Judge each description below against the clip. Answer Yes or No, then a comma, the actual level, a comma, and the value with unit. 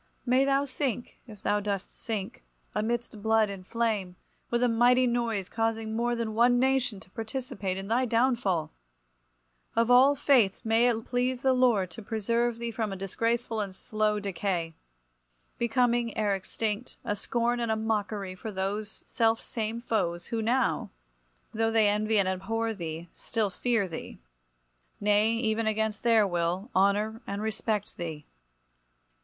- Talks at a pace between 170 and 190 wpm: No, average, 155 wpm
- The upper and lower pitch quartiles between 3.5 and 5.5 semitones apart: No, average, 2.9 semitones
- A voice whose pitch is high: Yes, high, 220 Hz